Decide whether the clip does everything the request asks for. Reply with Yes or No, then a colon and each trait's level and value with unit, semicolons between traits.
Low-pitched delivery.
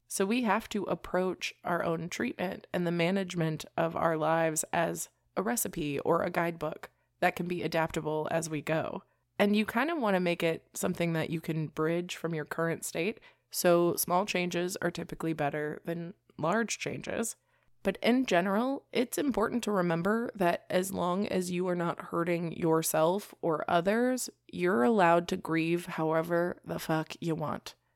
No: medium, 170 Hz